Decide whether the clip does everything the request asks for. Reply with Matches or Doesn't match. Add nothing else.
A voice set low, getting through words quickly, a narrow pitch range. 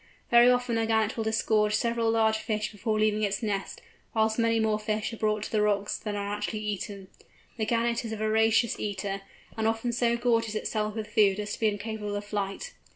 Doesn't match